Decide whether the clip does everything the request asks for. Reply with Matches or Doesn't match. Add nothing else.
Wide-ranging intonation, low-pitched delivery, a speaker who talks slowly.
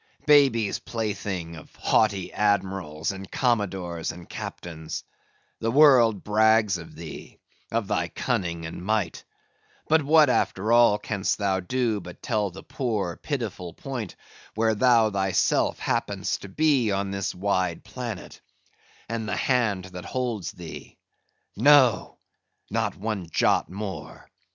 Doesn't match